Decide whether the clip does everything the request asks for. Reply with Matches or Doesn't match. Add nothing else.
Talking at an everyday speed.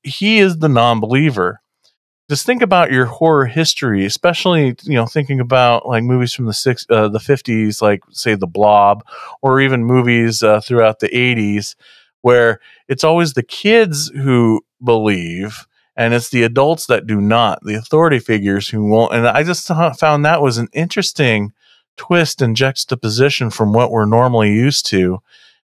Matches